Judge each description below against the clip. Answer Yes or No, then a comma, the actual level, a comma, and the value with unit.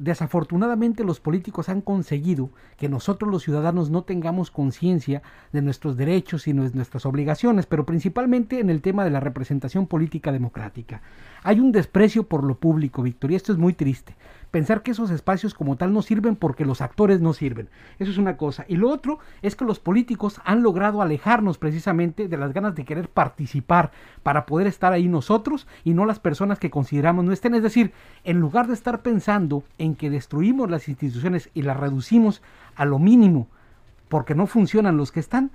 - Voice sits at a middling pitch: Yes, medium, 170 Hz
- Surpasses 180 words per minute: Yes, fast, 190 wpm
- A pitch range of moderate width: No, wide, 6.2 semitones